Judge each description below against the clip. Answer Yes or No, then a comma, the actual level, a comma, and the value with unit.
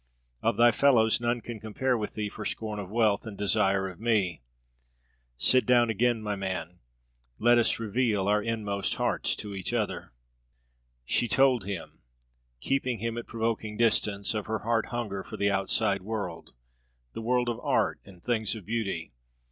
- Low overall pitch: Yes, low, 110 Hz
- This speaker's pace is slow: No, average, 165 wpm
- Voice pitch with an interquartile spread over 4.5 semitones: No, average, 2.9 semitones